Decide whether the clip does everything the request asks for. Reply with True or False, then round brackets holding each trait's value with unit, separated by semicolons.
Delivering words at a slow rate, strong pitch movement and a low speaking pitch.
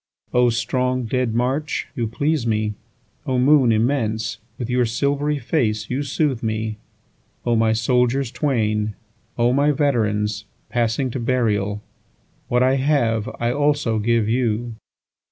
False (120 wpm; 3.1 semitones; 120 Hz)